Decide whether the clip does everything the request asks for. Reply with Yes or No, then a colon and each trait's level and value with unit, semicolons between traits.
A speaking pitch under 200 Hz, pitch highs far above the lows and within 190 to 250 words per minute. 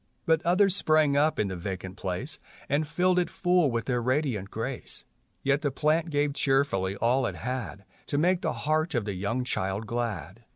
Yes: low, 135 Hz; wide, 6.5 semitones; average, 200 wpm